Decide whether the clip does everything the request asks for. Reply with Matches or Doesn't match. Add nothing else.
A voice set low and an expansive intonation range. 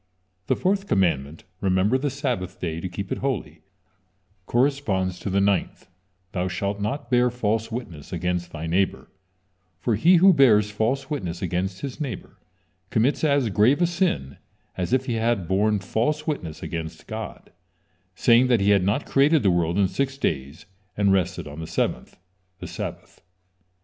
Matches